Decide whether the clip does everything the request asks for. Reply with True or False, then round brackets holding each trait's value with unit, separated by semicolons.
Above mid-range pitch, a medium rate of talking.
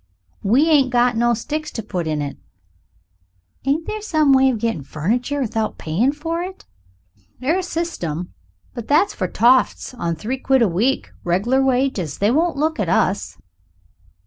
True (250 Hz; 160 wpm)